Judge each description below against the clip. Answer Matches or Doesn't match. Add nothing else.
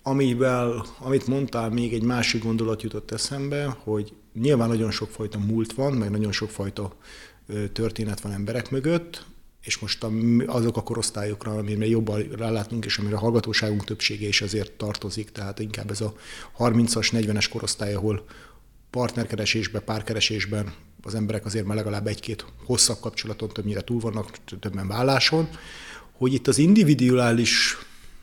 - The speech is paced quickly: Doesn't match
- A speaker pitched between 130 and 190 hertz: Doesn't match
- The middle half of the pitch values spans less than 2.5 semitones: Matches